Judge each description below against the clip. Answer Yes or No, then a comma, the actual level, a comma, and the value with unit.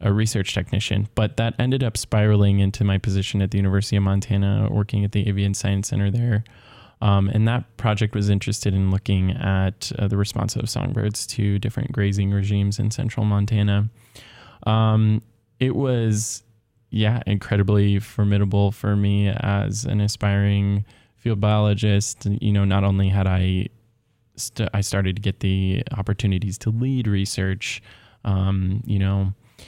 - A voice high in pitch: No, low, 105 Hz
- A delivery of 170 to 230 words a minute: No, average, 155 wpm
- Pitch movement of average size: No, narrow, 2.1 semitones